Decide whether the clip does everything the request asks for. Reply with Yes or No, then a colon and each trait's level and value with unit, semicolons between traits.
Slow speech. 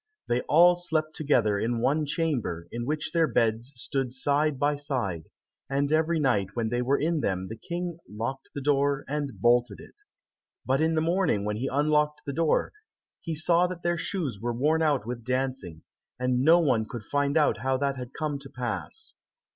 No: average, 190 wpm